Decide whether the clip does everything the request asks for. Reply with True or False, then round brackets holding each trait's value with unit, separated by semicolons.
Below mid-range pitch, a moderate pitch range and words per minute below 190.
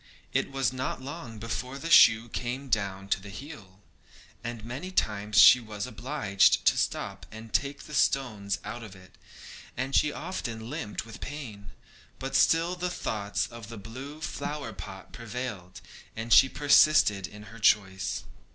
True (115 Hz; 4.9 semitones; 160 wpm)